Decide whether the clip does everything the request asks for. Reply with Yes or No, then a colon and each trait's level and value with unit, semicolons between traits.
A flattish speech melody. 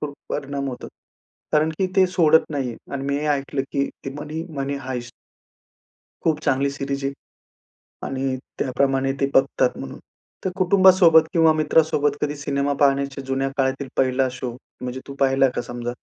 Yes: narrow, 2.1 semitones